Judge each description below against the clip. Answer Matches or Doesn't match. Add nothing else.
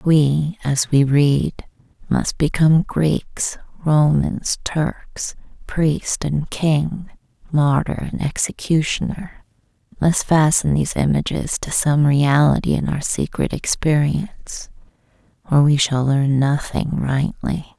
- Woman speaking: Matches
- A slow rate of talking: Matches